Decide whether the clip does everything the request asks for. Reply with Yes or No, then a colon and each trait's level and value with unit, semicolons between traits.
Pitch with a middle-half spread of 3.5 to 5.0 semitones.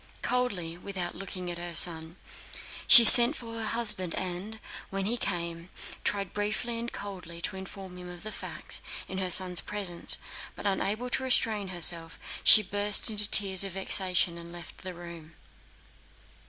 No: average, 3.1 semitones